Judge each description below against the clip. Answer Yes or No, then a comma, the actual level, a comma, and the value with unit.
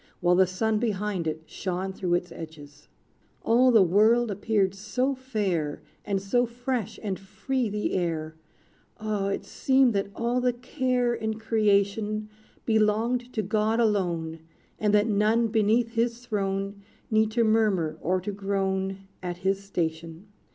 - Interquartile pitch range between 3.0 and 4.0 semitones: Yes, average, 3.3 semitones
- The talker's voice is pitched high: Yes, high, 210 Hz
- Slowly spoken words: No, average, 145 wpm